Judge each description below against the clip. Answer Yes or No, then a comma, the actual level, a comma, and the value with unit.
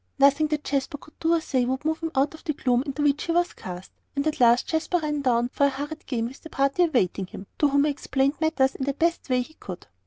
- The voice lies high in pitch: Yes, very high, 280 Hz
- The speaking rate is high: Yes, fast, 270 wpm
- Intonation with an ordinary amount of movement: Yes, average, 3.3 semitones